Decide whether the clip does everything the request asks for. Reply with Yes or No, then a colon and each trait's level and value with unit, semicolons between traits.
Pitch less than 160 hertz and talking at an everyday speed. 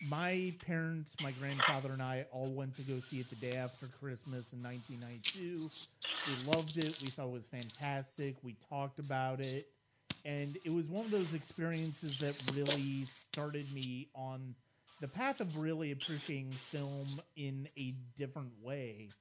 Yes: medium, 140 Hz; average, 160 wpm